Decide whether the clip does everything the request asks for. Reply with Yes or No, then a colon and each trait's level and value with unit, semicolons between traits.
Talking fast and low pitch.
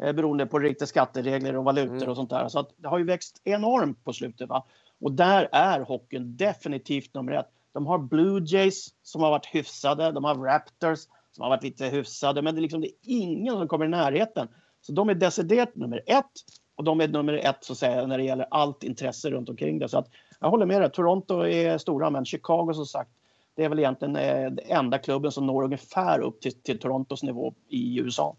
No: fast, 220 wpm; medium, 145 Hz